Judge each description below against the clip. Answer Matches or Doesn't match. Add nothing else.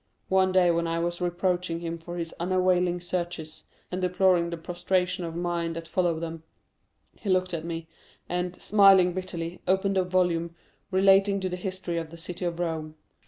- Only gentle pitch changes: Matches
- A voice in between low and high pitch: Matches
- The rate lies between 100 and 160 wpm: Doesn't match